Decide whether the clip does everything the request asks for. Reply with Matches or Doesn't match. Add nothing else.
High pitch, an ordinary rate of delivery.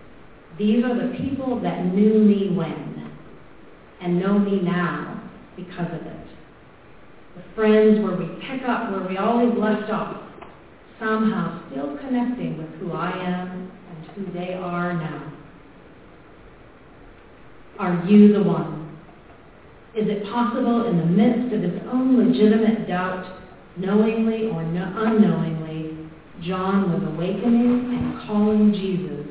Doesn't match